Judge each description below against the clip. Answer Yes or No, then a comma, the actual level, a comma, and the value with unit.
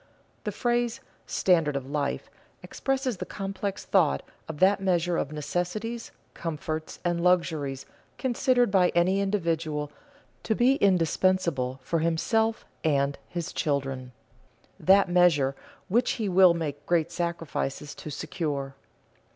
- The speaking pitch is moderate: Yes, medium, 170 Hz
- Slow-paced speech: Yes, slow, 125 wpm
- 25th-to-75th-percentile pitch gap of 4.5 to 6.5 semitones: Yes, average, 4.8 semitones